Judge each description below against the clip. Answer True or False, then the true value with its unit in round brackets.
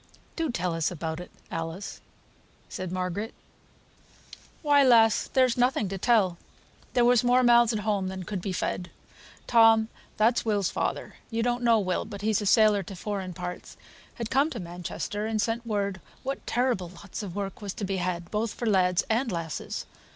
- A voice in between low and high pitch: False (210 Hz)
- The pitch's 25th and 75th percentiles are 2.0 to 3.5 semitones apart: False (4.2 semitones)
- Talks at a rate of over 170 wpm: True (180 wpm)